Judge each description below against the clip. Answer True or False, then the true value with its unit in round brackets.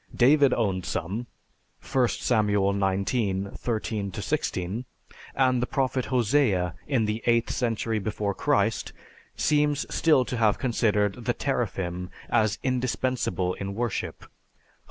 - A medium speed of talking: False (120 wpm)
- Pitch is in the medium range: False (110 Hz)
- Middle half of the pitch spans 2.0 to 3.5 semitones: False (4.3 semitones)